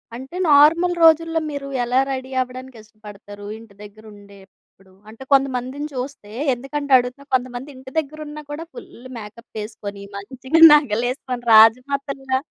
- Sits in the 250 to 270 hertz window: Yes, very high, 255 Hz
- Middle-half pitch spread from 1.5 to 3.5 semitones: No, average, 4.2 semitones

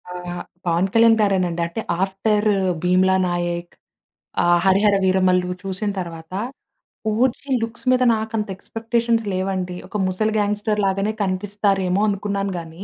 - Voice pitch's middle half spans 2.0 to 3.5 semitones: Yes, average, 2.9 semitones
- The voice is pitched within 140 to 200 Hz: Yes, high, 195 Hz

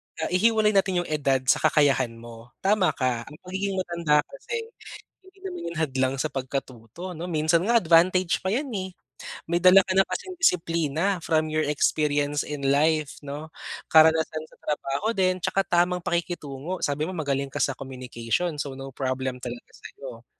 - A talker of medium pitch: Yes, medium, 160 Hz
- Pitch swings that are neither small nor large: Yes, average, 5.0 semitones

